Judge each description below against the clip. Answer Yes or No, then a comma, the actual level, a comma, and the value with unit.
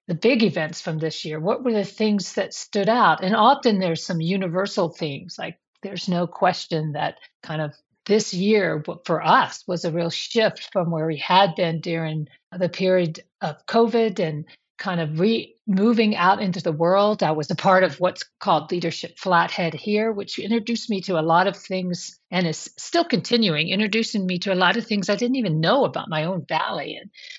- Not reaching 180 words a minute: No, average, 200 wpm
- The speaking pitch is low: No, medium, 185 Hz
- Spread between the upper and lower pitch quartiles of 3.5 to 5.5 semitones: Yes, average, 4.1 semitones